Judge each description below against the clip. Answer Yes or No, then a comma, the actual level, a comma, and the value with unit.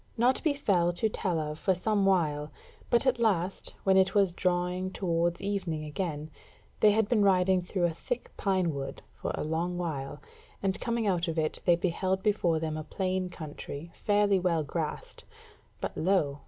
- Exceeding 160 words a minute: Yes, average, 175 wpm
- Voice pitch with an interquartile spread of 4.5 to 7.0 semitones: No, average, 3.4 semitones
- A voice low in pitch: No, medium, 180 Hz